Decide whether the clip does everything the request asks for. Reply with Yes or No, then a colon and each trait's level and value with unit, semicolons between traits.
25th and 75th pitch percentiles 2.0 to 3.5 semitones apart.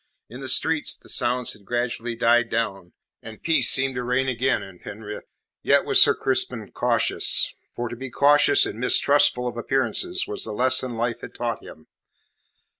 Yes: narrow, 2.5 semitones